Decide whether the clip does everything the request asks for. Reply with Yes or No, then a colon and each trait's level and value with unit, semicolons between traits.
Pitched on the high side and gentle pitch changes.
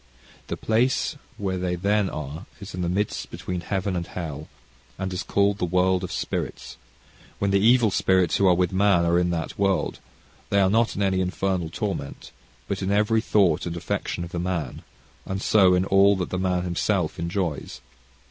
No: very low, 95 Hz; narrow, 2.2 semitones